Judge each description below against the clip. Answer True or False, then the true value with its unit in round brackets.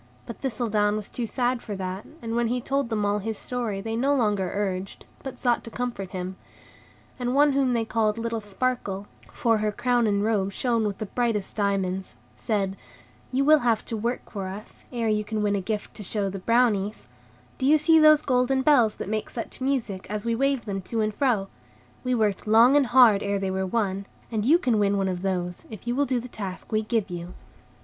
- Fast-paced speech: True (220 wpm)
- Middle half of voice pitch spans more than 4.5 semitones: False (3.6 semitones)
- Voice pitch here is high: True (220 Hz)